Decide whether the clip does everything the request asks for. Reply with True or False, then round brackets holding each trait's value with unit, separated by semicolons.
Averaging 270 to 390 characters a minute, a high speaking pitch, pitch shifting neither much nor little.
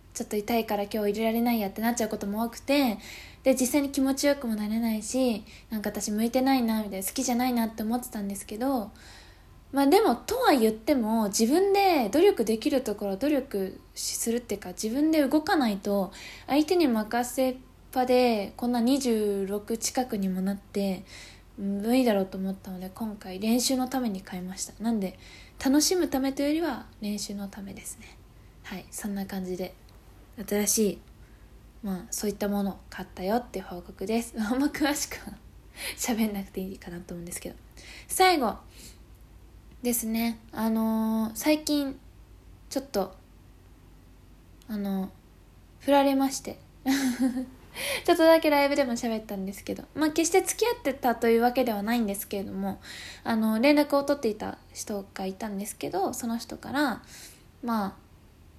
True (340 characters per minute; 225 Hz; 4.9 semitones)